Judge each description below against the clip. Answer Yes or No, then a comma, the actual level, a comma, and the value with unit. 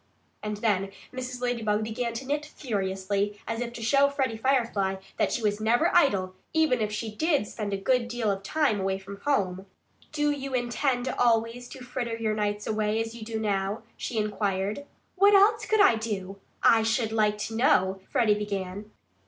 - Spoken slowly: No, average, 185 wpm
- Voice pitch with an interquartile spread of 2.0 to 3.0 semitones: No, average, 3.4 semitones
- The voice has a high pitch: Yes, high, 225 Hz